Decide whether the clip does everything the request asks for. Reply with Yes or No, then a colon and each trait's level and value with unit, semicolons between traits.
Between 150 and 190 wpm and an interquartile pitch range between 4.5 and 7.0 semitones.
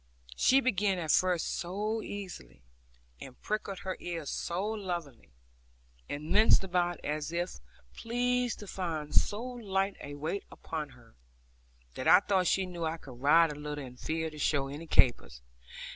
Yes: average, 160 wpm; average, 5.2 semitones